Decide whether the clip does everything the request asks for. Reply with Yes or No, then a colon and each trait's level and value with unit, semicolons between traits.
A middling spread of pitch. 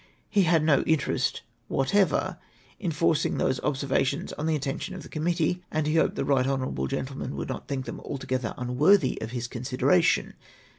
Yes: average, 4.1 semitones